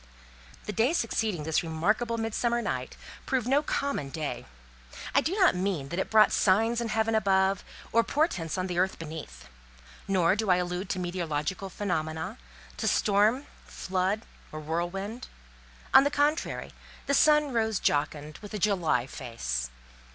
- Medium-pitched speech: No, high, 195 Hz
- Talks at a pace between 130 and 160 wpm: Yes, average, 150 wpm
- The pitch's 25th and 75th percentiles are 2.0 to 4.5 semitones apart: No, wide, 5.6 semitones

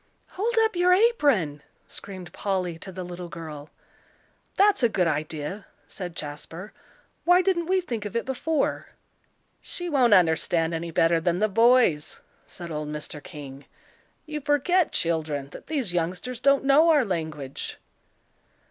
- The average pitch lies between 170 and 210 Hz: Yes, medium, 185 Hz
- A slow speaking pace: No, average, 145 wpm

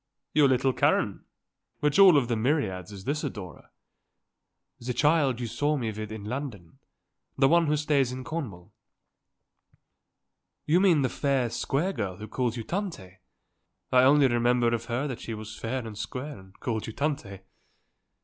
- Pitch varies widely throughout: No, average, 5.0 semitones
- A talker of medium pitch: No, low, 125 Hz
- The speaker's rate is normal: Yes, average, 165 wpm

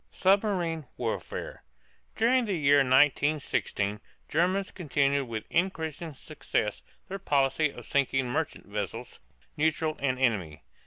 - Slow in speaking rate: Yes, slow, 110 wpm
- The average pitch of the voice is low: No, medium, 145 Hz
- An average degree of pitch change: Yes, average, 4.6 semitones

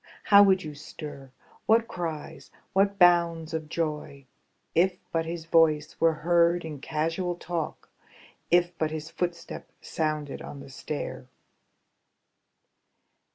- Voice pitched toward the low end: No, medium, 165 Hz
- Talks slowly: Yes, slow, 120 wpm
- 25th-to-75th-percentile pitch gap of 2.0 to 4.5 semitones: Yes, narrow, 2.4 semitones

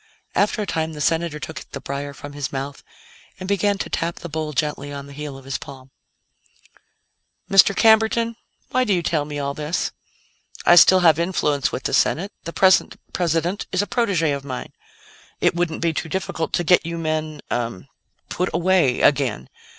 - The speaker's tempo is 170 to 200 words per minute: Yes, average, 185 wpm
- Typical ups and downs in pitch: Yes, average, 4.3 semitones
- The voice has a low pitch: No, medium, 160 Hz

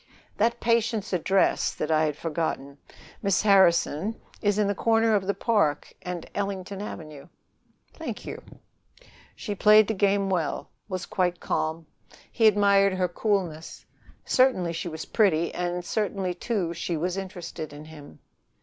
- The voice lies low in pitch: No, medium, 185 Hz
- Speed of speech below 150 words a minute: Yes, average, 140 wpm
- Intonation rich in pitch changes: No, average, 3.7 semitones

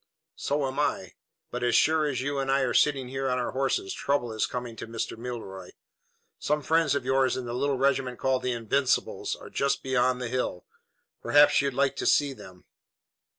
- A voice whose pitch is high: No, low, 130 Hz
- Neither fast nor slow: Yes, average, 195 wpm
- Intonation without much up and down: Yes, narrow, 2.2 semitones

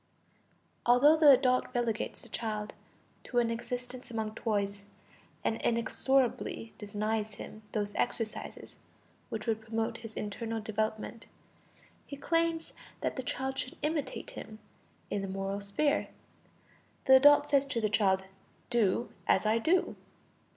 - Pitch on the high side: Yes, high, 230 Hz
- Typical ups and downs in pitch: Yes, average, 3.6 semitones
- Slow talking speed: Yes, slow, 130 wpm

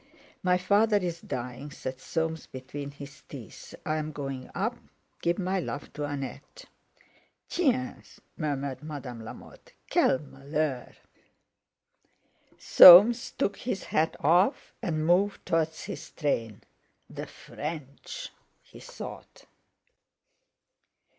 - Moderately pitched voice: Yes, medium, 155 Hz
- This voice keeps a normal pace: No, slow, 105 wpm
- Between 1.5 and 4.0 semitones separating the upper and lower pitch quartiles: No, average, 5.0 semitones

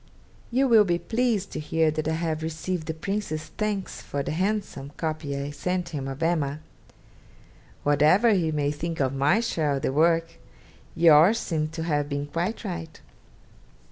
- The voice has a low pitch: No, medium, 160 Hz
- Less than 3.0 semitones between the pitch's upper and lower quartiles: No, average, 3.6 semitones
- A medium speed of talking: Yes, average, 170 wpm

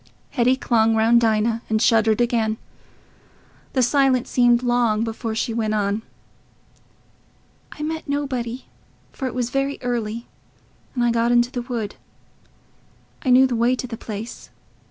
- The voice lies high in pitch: Yes, high, 235 Hz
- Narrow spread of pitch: Yes, narrow, 2.1 semitones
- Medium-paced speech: Yes, average, 145 wpm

